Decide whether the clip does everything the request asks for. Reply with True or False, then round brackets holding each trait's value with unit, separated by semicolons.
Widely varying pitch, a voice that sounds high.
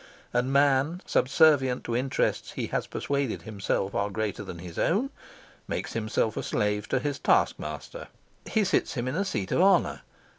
False (6.1 semitones; 130 Hz)